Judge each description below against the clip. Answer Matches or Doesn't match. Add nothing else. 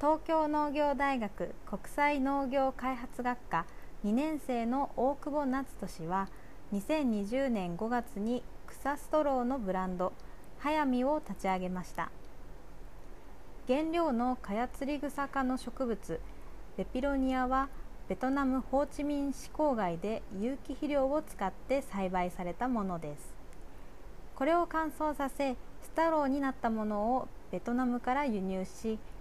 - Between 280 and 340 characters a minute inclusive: Doesn't match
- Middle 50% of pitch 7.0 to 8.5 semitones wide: Doesn't match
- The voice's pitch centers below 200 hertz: Doesn't match